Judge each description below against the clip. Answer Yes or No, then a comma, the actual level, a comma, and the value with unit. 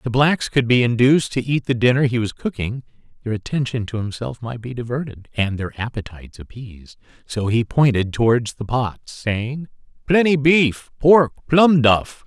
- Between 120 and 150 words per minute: No, average, 175 wpm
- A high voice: No, low, 125 Hz